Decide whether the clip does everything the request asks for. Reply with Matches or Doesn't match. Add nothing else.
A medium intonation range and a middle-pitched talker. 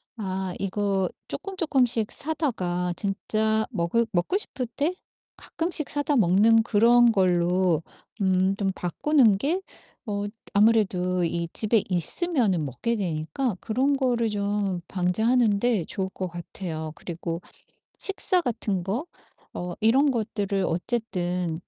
Doesn't match